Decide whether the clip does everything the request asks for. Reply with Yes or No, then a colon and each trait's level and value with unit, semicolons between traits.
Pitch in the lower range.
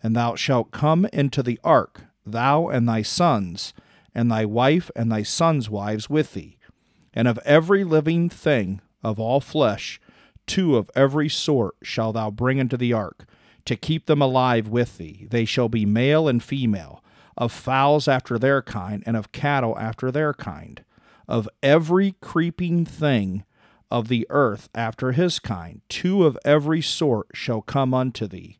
Yes: low, 125 Hz